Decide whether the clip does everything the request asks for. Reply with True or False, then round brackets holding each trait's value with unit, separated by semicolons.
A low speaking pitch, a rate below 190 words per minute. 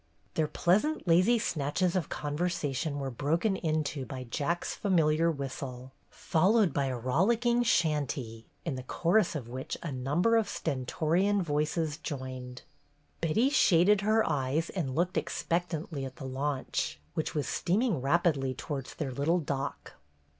False (155 Hz; 140 wpm)